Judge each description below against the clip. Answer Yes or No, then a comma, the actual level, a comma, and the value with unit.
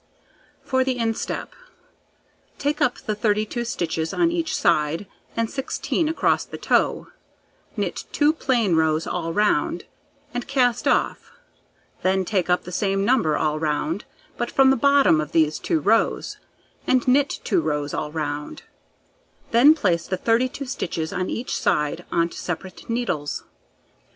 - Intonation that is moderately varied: No, wide, 7.8 semitones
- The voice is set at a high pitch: Yes, high, 205 Hz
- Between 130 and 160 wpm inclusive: Yes, average, 145 wpm